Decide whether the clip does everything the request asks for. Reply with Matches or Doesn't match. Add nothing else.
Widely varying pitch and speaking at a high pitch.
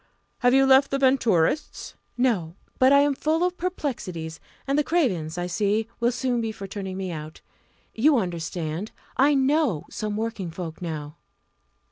Matches